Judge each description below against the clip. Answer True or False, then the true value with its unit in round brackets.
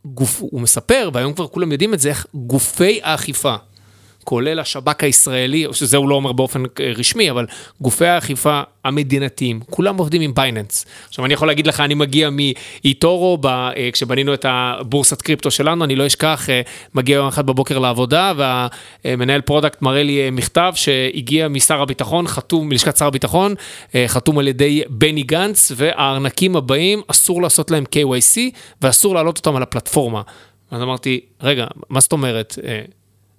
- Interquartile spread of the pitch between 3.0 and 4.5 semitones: True (3.3 semitones)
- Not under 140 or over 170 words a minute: True (150 wpm)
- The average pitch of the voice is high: False (140 Hz)